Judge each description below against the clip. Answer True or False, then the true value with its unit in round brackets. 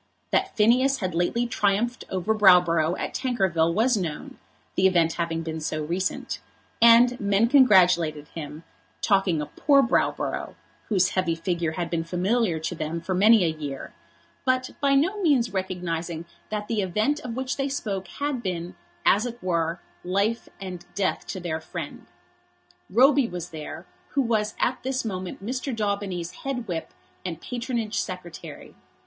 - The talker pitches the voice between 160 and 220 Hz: True (190 Hz)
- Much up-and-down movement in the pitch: True (5.7 semitones)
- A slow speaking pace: False (155 wpm)